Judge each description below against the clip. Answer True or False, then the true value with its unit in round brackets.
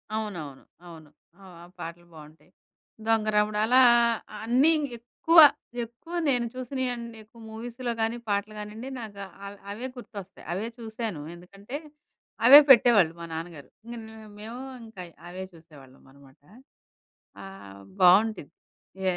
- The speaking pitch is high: True (210 Hz)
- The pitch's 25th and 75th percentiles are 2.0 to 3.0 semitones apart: False (5.2 semitones)